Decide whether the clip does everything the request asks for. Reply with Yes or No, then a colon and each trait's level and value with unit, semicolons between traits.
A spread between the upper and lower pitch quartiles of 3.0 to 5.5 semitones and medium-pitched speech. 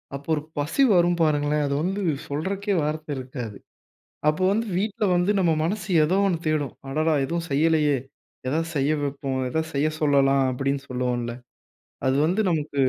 Yes: average, 3.8 semitones; medium, 150 Hz